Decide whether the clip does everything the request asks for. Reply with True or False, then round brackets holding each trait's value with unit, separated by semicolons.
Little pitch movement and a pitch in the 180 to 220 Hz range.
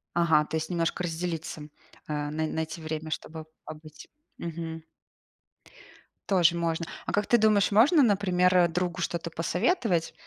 False (2.3 semitones; 170 Hz)